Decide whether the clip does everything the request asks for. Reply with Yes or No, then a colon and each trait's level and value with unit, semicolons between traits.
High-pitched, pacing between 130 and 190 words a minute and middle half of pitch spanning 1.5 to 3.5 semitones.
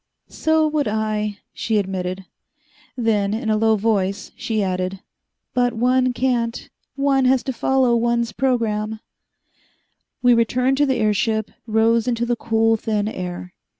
Yes: high, 225 Hz; average, 145 wpm; average, 2.8 semitones